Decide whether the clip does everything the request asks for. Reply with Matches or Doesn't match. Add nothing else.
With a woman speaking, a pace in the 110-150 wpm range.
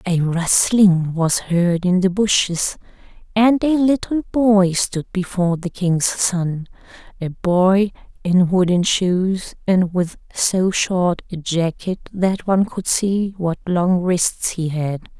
Matches